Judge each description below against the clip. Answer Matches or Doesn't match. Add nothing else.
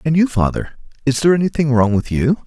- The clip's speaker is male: Matches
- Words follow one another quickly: Doesn't match